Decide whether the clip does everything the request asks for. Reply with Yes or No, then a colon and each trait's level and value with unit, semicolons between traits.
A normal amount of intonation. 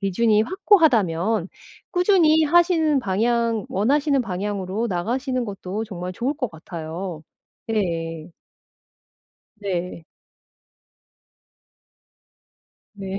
No: wide, 6.4 semitones